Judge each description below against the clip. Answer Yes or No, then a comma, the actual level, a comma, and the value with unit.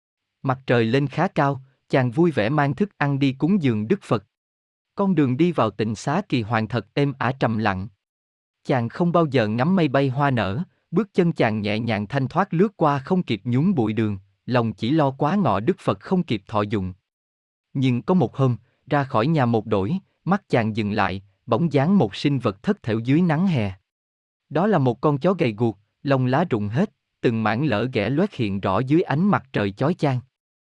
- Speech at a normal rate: Yes, average, 215 wpm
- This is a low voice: Yes, low, 130 Hz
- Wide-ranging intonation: Yes, wide, 6.7 semitones